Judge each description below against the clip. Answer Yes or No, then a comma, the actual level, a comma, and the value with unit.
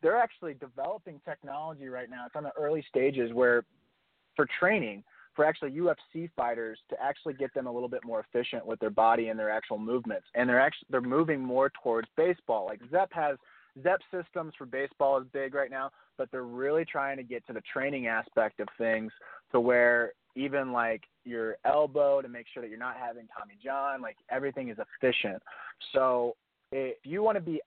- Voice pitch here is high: No, low, 135 Hz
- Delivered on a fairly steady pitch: No, average, 3.7 semitones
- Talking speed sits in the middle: Yes, average, 195 wpm